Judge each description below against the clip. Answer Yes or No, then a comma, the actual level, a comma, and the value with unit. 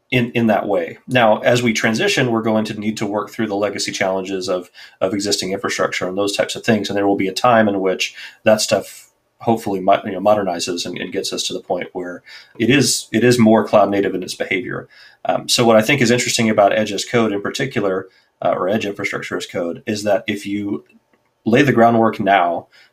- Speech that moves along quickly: Yes, fast, 225 wpm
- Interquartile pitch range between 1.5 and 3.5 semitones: Yes, narrow, 2.5 semitones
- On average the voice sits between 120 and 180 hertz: No, low, 105 Hz